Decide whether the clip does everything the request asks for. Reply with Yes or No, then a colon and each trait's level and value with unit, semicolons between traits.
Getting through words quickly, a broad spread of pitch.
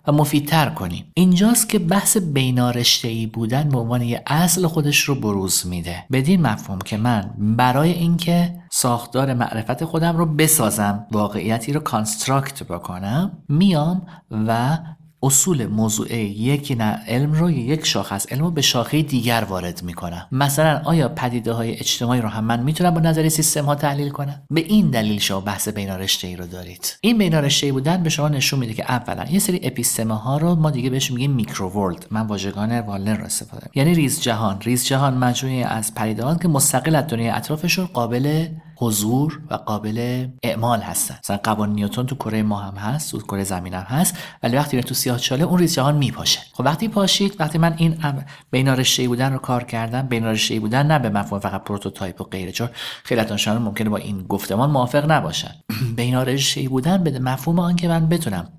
Yes: fast, 180 wpm; wide, 6.0 semitones